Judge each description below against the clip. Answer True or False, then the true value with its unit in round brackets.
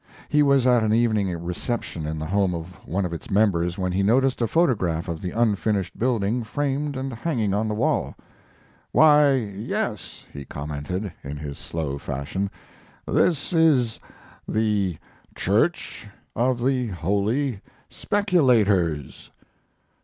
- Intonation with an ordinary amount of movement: False (6.2 semitones)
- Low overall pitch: True (105 Hz)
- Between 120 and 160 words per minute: True (135 wpm)